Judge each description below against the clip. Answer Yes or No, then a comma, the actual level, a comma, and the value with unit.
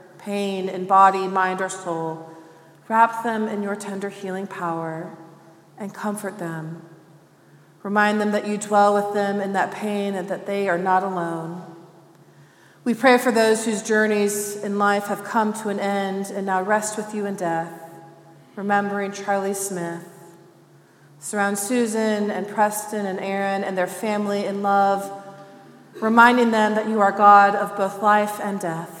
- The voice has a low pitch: No, high, 200 Hz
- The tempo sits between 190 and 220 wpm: No, average, 160 wpm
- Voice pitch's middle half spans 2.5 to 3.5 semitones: Yes, average, 3.2 semitones